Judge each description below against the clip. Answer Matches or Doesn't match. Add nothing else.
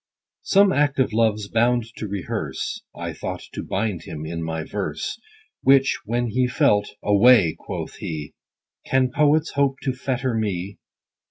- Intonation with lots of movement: Doesn't match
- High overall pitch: Doesn't match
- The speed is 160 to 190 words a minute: Doesn't match